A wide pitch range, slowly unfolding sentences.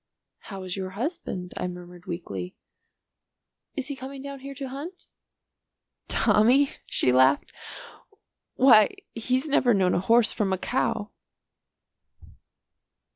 Yes: wide, 7.0 semitones; slow, 120 wpm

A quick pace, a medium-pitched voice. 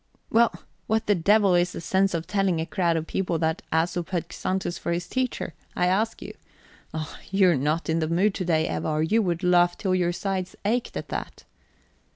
Yes: fast, 210 wpm; medium, 180 Hz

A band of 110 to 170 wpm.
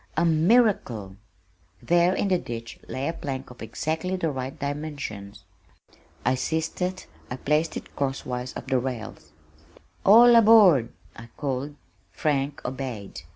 Yes: average, 140 wpm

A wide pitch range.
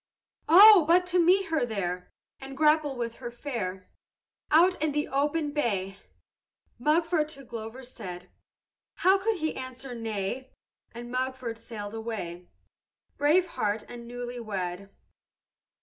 Yes: wide, 5.8 semitones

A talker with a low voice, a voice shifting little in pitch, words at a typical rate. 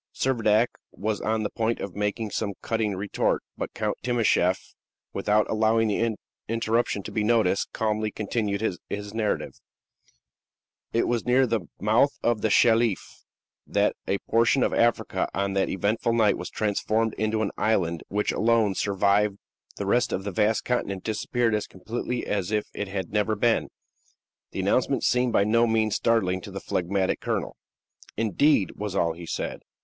Yes: low, 110 Hz; narrow, 2.3 semitones; average, 160 wpm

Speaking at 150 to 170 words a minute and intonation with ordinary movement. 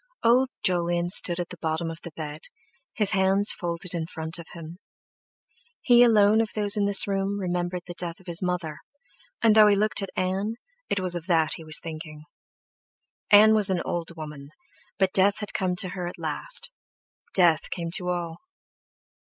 No: average, 180 wpm; average, 3.2 semitones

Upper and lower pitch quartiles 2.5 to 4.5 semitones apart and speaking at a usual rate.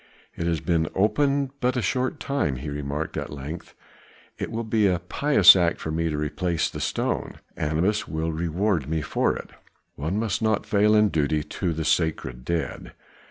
No: wide, 5.5 semitones; average, 180 wpm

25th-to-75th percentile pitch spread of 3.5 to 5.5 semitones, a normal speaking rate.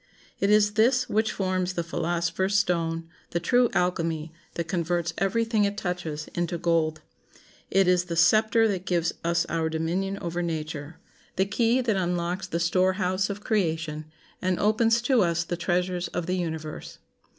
No: average, 3.0 semitones; average, 160 wpm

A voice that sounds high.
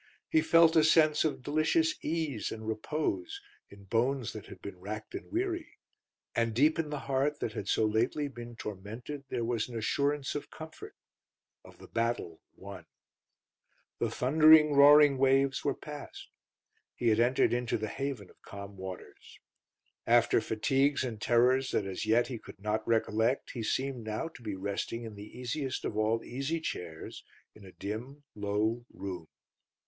No: low, 120 Hz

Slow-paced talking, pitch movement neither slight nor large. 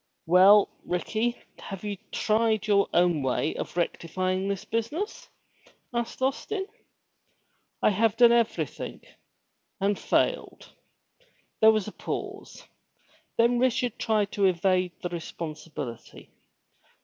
Yes: slow, 110 wpm; average, 4.3 semitones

